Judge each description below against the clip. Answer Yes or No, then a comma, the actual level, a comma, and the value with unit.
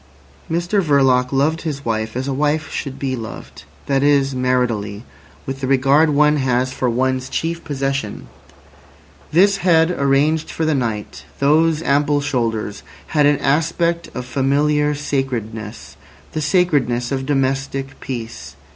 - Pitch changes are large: No, average, 2.9 semitones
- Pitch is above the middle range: No, low, 135 Hz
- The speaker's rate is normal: No, slow, 130 wpm